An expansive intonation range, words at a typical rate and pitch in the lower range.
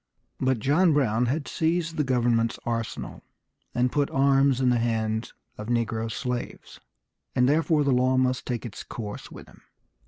No: average, 3.2 semitones; average, 160 wpm; low, 125 Hz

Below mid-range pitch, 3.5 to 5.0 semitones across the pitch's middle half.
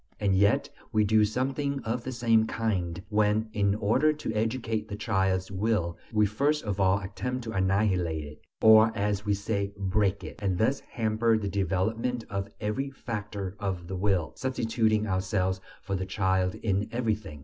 No: low, 105 Hz; average, 2.8 semitones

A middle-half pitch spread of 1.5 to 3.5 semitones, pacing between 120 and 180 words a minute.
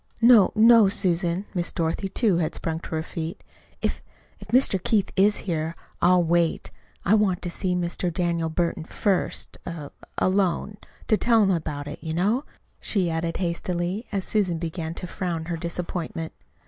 Yes: average, 3.0 semitones; average, 170 wpm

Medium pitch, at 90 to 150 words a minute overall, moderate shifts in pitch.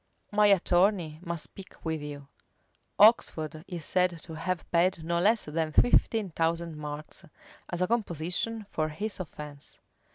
Yes: medium, 170 Hz; average, 140 wpm; average, 3.5 semitones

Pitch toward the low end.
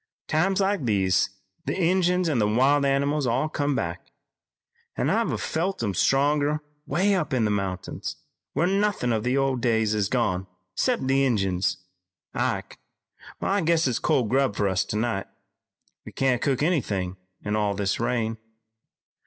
Yes: low, 130 Hz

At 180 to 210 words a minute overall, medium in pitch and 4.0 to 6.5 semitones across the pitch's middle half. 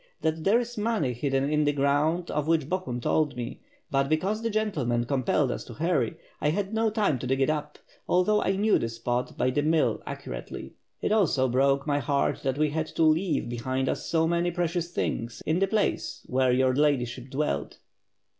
Yes: average, 200 wpm; medium, 150 Hz; average, 5.1 semitones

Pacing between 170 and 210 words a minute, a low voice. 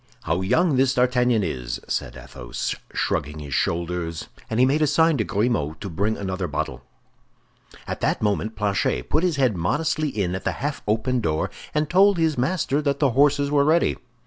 Yes: average, 185 wpm; low, 120 Hz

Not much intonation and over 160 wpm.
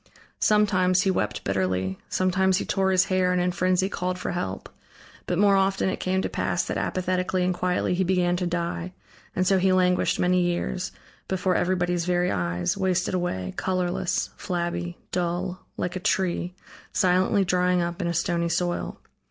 Yes: narrow, 1.1 semitones; average, 170 wpm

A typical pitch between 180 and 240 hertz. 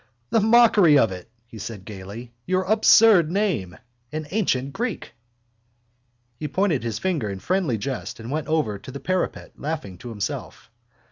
No: medium, 145 Hz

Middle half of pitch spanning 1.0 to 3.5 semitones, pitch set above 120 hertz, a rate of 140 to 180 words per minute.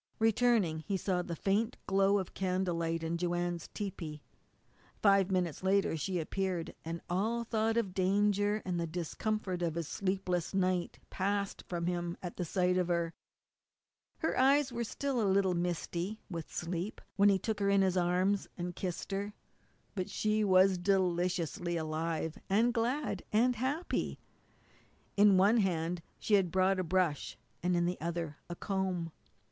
Yes: average, 2.8 semitones; medium, 185 Hz; average, 155 wpm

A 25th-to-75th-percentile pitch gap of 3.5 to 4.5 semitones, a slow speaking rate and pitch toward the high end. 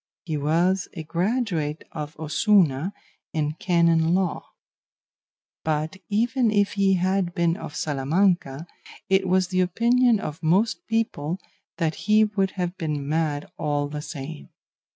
No: average, 4.1 semitones; slow, 130 wpm; medium, 175 Hz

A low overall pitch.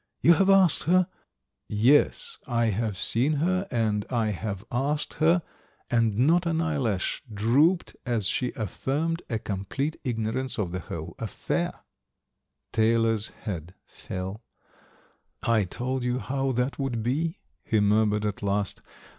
Yes: low, 120 Hz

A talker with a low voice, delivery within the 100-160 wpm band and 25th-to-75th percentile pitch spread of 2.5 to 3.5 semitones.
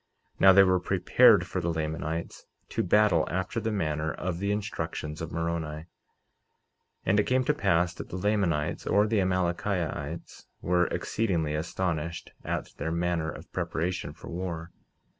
Yes: very low, 85 Hz; average, 155 wpm; average, 3.1 semitones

